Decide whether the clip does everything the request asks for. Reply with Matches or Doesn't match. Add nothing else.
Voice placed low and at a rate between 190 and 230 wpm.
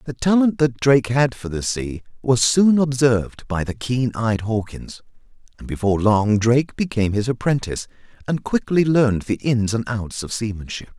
Doesn't match